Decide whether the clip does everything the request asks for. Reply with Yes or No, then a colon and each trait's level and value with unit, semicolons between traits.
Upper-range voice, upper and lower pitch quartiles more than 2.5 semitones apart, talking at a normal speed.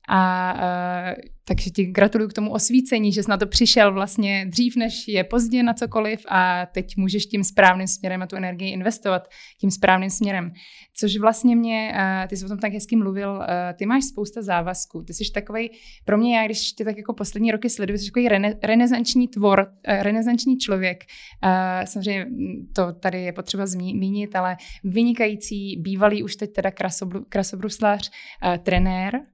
No: high, 205 Hz; average, 2.9 semitones; fast, 175 wpm